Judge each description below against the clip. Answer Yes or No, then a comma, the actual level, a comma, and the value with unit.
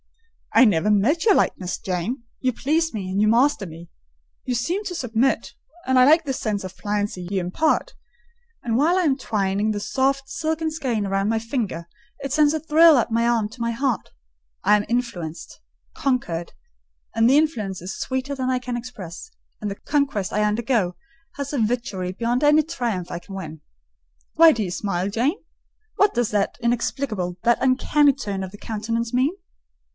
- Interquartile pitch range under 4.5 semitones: No, wide, 5.6 semitones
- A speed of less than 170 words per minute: No, average, 175 wpm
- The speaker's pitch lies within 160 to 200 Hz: No, high, 235 Hz